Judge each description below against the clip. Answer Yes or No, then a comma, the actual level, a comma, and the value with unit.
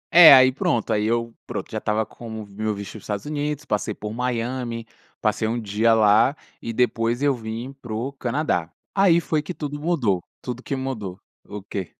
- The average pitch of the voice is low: Yes, low, 115 Hz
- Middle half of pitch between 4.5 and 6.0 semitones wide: No, average, 4.1 semitones